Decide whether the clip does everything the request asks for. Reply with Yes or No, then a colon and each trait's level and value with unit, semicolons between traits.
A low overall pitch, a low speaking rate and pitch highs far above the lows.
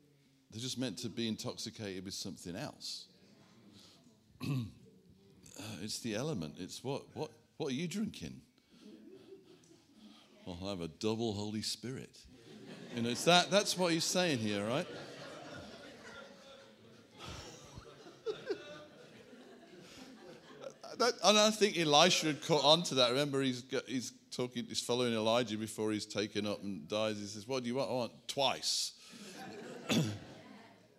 Yes: low, 125 Hz; slow, 130 wpm; wide, 6.4 semitones